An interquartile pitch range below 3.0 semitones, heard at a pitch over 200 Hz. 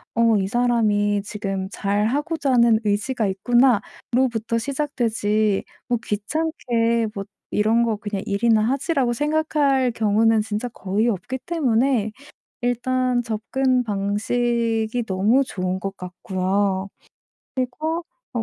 No: average, 3.3 semitones; high, 225 Hz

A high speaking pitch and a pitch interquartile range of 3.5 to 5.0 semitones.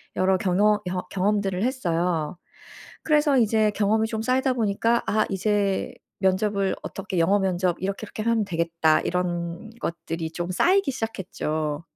Yes: high, 195 Hz; average, 3.8 semitones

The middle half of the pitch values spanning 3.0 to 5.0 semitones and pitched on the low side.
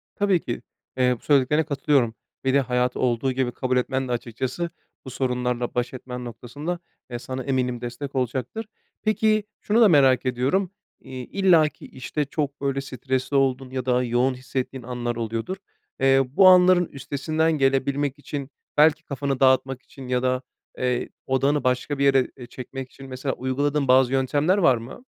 No: narrow, 2.4 semitones; low, 130 Hz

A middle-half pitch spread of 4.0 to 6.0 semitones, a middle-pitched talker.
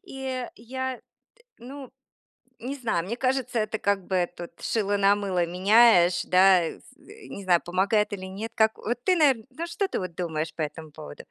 No: wide, 5.5 semitones; high, 205 Hz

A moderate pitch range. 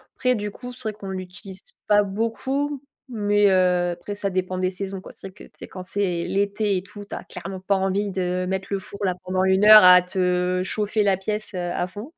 No: narrow, 2.1 semitones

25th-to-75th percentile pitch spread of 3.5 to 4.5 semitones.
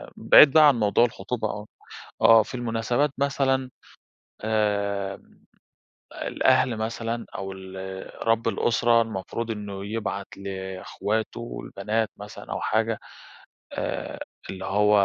No: average, 2.9 semitones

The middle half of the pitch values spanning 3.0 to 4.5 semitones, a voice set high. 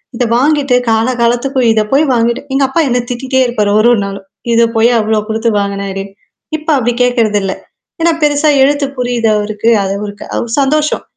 Yes: average, 3.8 semitones; high, 235 Hz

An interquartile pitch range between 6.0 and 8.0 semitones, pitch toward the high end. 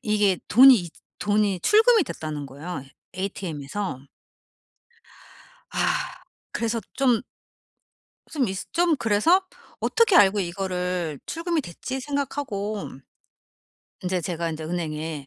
Yes: wide, 7.5 semitones; high, 195 Hz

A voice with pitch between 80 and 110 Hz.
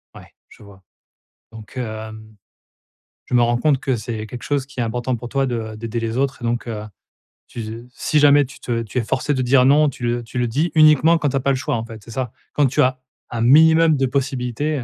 No: low, 125 Hz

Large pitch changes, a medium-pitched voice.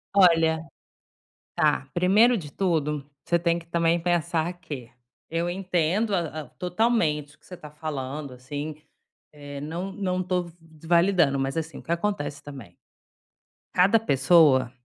No: average, 3.5 semitones; medium, 165 Hz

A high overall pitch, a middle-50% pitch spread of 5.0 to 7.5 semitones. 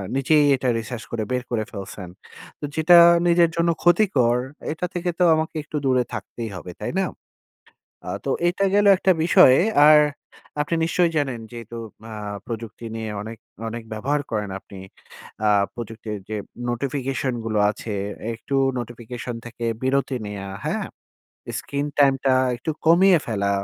No: low, 125 Hz; average, 5.3 semitones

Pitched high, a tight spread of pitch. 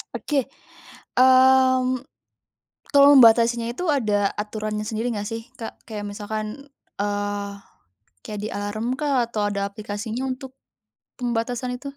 No: high, 230 Hz; average, 3.6 semitones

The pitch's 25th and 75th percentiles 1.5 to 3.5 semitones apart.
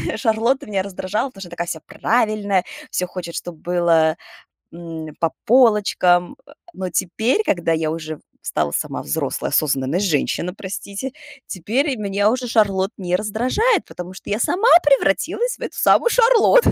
No: wide, 5.6 semitones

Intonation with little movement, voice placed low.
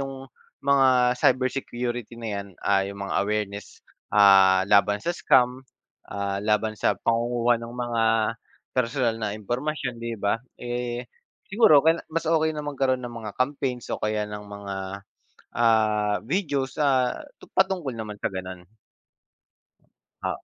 No: average, 4.1 semitones; low, 120 Hz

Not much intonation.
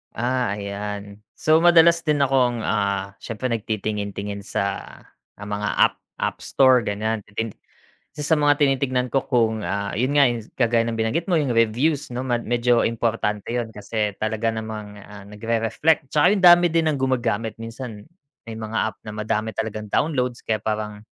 No: average, 3.6 semitones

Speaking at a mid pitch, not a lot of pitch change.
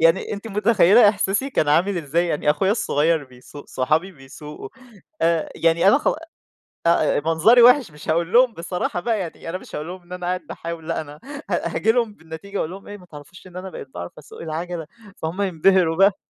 No: medium, 175 Hz; average, 3.8 semitones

